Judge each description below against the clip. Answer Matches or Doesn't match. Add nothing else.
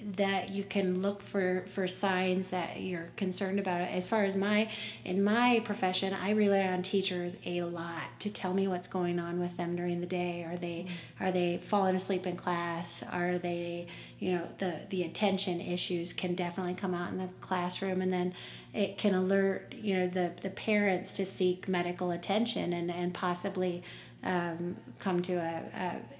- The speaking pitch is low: Doesn't match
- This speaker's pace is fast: Doesn't match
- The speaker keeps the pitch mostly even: Matches